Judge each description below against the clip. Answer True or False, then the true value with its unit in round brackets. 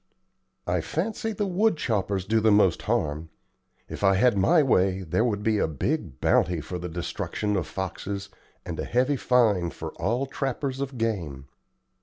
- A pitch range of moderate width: False (6.3 semitones)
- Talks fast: False (170 wpm)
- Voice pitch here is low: True (105 Hz)